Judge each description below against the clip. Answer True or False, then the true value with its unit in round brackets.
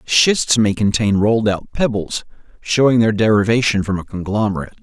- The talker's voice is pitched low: True (105 Hz)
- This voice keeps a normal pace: True (150 wpm)